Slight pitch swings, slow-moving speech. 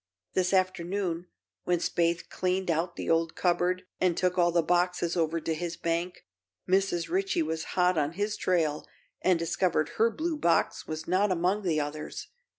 No: narrow, 2.0 semitones; average, 165 wpm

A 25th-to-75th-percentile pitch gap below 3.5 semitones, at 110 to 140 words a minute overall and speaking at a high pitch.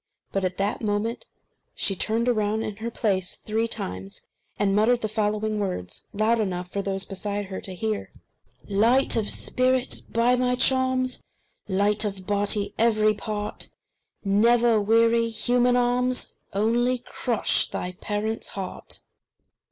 Yes: average, 2.7 semitones; slow, 135 wpm; high, 215 Hz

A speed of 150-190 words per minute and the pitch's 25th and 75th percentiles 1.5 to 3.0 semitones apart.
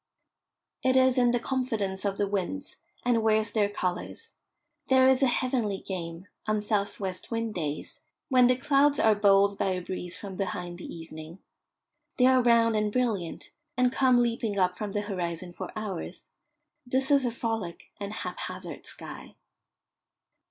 No: average, 160 wpm; average, 4.8 semitones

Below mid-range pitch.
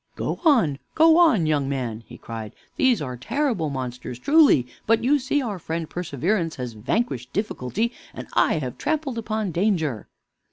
No: medium, 175 Hz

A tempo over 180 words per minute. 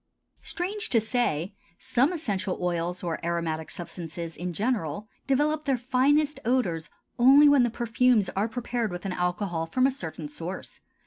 No: average, 150 wpm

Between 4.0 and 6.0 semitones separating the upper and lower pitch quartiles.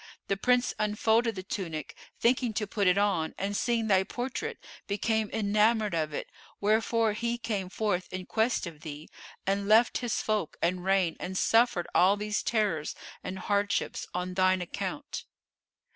No: average, 3.3 semitones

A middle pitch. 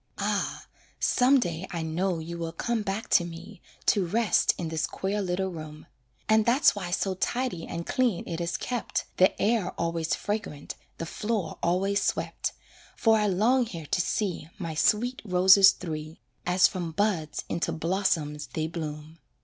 Yes: medium, 180 Hz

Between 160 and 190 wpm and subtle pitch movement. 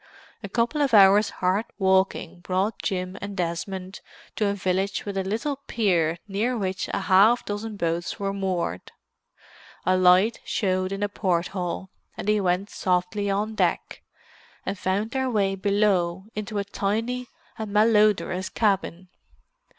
No: average, 150 wpm; narrow, 2.3 semitones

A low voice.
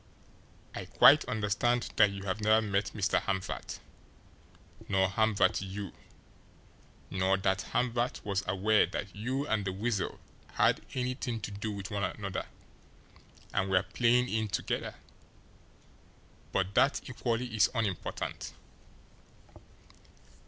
Yes: low, 105 Hz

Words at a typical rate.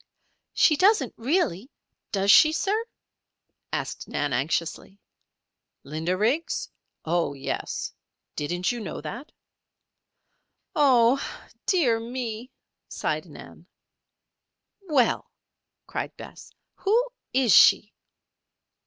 No: slow, 90 wpm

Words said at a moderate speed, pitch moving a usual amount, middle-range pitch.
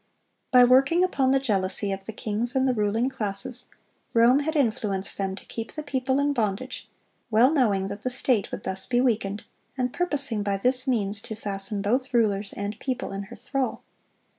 No: average, 190 wpm; average, 4.5 semitones; high, 235 Hz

